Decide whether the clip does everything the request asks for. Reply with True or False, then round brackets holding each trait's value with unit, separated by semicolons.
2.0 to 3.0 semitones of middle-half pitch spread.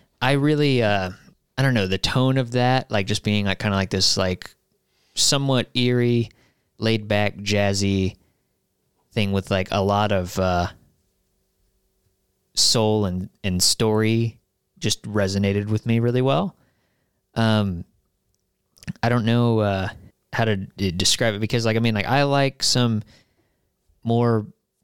False (3.7 semitones)